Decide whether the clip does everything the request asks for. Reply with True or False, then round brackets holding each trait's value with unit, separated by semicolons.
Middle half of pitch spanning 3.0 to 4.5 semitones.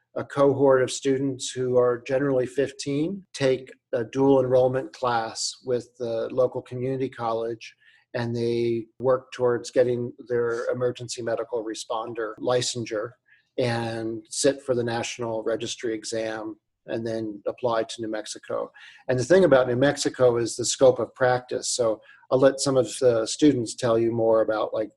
False (2.5 semitones)